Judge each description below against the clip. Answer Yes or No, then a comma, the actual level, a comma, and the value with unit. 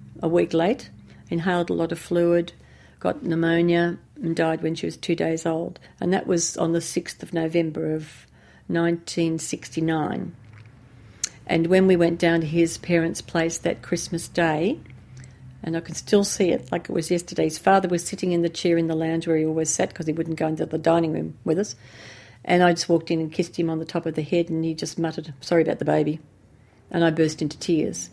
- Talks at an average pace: No, fast, 215 wpm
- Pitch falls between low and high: Yes, medium, 165 Hz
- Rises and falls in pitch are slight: Yes, narrow, 1.3 semitones